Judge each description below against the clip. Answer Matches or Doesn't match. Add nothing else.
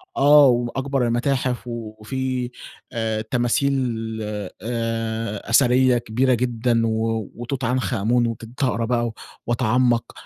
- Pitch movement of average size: Doesn't match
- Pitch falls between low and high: Doesn't match